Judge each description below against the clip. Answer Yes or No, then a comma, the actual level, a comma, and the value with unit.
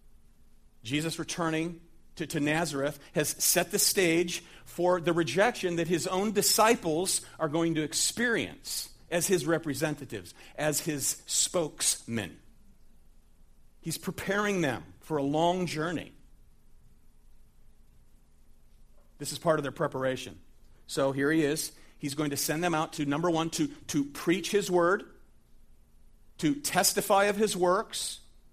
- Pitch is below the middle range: No, medium, 160 Hz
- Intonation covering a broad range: No, average, 3.6 semitones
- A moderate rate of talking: No, slow, 130 wpm